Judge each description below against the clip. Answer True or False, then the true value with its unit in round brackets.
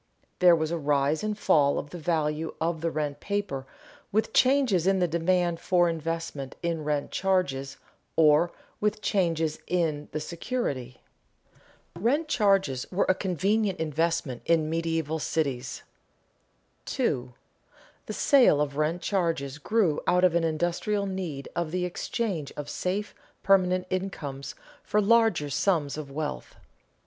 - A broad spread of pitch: False (4.2 semitones)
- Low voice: False (165 Hz)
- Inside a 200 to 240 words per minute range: False (140 wpm)